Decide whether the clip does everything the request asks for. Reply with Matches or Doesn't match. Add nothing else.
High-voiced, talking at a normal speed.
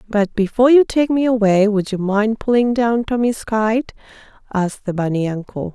Matches